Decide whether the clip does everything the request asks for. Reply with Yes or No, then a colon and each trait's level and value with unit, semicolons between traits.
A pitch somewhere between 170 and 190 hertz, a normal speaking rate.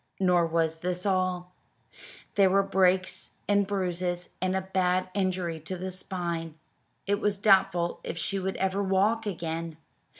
Yes: medium, 185 Hz; average, 145 wpm